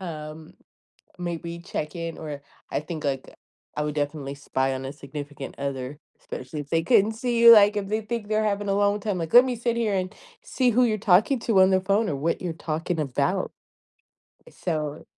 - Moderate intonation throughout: No, wide, 5.9 semitones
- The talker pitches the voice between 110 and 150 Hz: No, medium, 170 Hz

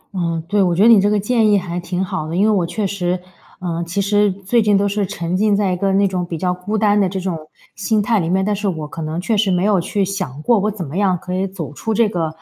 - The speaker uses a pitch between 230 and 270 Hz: No, high, 190 Hz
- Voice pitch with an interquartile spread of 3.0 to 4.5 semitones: No, narrow, 2.6 semitones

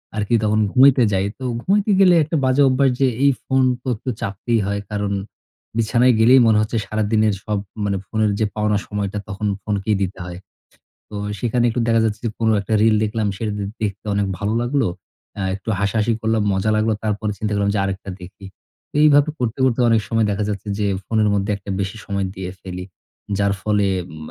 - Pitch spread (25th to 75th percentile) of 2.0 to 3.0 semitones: Yes, narrow, 2.4 semitones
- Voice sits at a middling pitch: No, low, 105 Hz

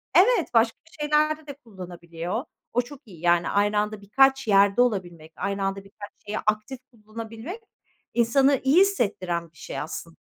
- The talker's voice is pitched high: Yes, high, 215 Hz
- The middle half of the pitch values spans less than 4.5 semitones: No, wide, 5.6 semitones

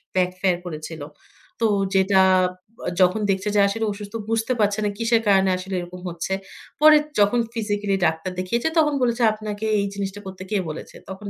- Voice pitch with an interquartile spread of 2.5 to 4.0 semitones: Yes, average, 2.9 semitones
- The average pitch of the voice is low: No, high, 200 Hz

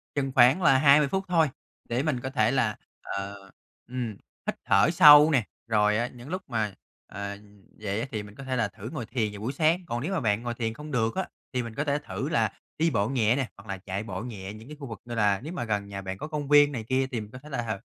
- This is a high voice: No, low, 120 Hz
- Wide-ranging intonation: No, average, 5.0 semitones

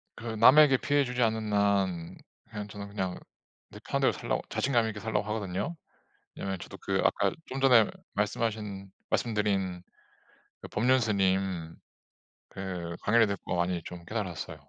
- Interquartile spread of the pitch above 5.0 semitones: No, average, 3.2 semitones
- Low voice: Yes, low, 105 Hz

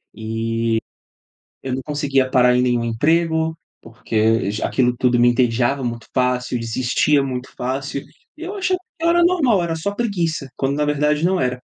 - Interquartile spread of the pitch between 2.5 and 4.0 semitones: No, average, 4.8 semitones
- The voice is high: No, low, 135 Hz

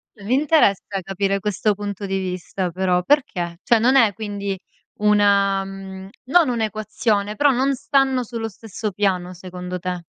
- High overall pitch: Yes, high, 200 Hz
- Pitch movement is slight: No, average, 3.1 semitones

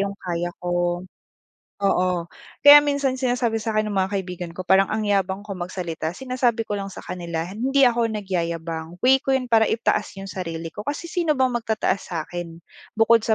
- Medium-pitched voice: No, high, 200 Hz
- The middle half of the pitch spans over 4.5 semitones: Yes, average, 5.2 semitones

